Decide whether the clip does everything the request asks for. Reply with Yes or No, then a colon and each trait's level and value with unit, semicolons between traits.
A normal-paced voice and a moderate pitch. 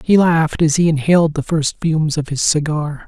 No: fast, 215 wpm; medium, 155 Hz